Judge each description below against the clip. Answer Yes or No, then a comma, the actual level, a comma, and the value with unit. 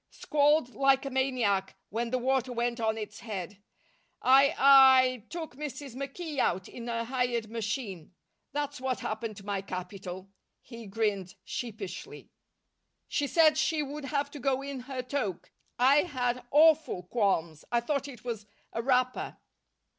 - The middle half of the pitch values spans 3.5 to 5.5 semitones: Yes, average, 4.3 semitones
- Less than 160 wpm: Yes, average, 150 wpm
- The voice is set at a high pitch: Yes, very high, 250 Hz